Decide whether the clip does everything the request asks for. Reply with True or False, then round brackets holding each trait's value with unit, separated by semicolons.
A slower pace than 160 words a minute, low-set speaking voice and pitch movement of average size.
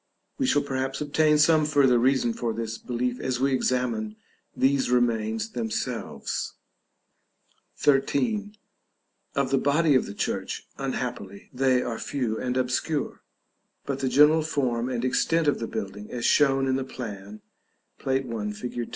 True (150 wpm; 130 Hz; 3.2 semitones)